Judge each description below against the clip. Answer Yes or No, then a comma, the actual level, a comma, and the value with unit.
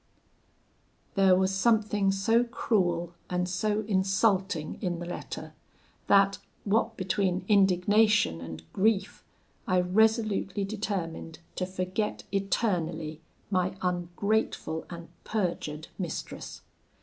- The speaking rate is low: Yes, slow, 100 wpm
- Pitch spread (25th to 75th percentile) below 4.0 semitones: Yes, average, 2.9 semitones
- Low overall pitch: No, high, 190 Hz